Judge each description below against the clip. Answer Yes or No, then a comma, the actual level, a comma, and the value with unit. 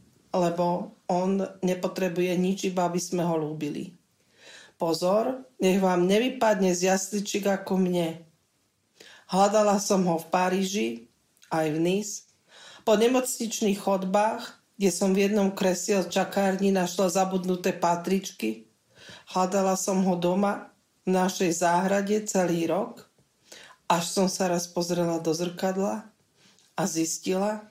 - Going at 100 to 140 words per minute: Yes, average, 120 wpm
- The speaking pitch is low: No, high, 190 Hz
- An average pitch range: No, narrow, 2.2 semitones